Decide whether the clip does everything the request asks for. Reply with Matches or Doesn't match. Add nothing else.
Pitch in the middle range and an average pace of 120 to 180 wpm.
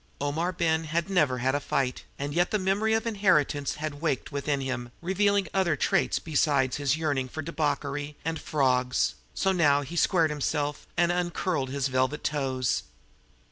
Matches